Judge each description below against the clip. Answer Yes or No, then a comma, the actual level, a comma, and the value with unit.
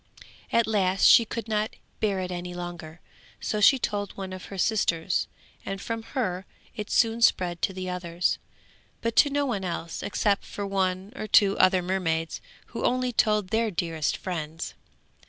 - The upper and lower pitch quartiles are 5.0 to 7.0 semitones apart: No, average, 3.4 semitones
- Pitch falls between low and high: No, high, 195 Hz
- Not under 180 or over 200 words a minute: No, average, 170 wpm